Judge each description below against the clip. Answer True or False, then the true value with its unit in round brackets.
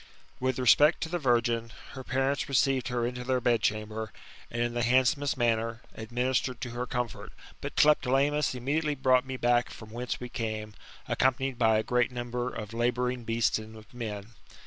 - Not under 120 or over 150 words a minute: False (175 wpm)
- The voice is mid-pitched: False (125 Hz)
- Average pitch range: False (2.1 semitones)